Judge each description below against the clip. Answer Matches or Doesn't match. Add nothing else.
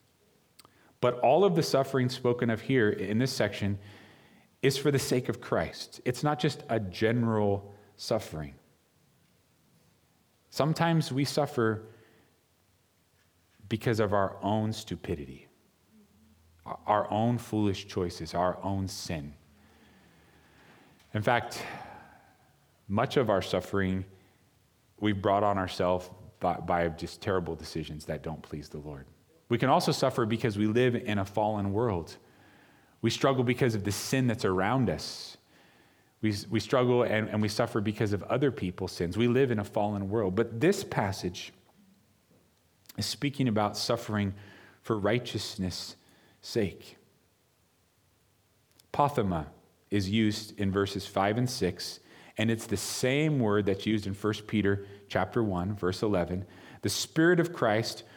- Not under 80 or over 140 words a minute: Matches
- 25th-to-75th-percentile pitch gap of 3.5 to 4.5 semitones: Matches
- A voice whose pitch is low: Matches